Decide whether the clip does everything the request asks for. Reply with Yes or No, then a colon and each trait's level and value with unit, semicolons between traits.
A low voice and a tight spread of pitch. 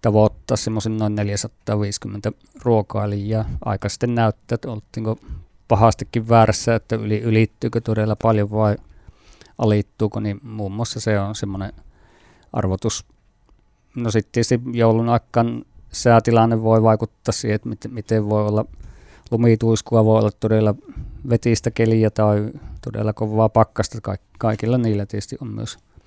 Yes: low, 110 Hz; narrow, 1.6 semitones